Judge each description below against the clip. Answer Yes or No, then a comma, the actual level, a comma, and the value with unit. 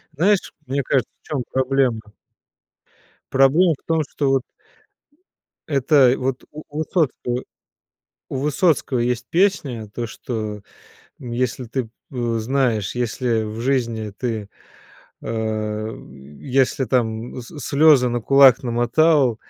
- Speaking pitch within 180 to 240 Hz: No, low, 125 Hz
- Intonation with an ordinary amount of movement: Yes, average, 3.1 semitones